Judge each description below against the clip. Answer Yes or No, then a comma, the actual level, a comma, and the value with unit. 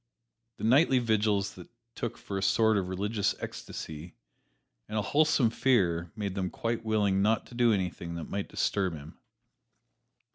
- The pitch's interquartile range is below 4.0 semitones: Yes, average, 3.4 semitones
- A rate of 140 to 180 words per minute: Yes, average, 155 wpm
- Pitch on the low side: Yes, low, 100 Hz